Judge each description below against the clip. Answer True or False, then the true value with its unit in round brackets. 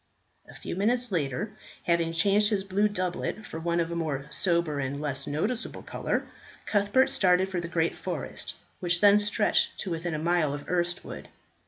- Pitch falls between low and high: True (175 Hz)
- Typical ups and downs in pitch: True (4.0 semitones)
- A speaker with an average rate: True (170 wpm)